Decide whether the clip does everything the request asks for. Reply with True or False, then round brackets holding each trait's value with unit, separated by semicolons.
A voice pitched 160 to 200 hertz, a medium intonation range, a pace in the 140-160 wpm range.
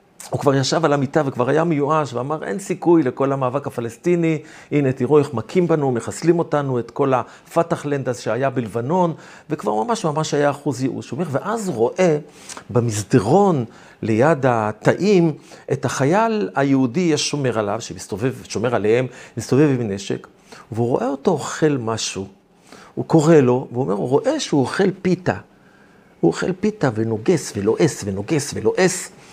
False (140 Hz; 4.8 semitones; 150 wpm)